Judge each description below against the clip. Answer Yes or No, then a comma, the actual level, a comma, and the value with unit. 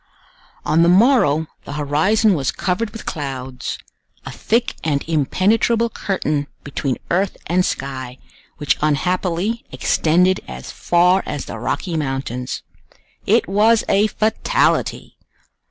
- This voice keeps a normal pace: No, slow, 115 wpm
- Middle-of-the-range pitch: Yes, medium, 175 Hz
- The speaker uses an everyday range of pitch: No, wide, 6.5 semitones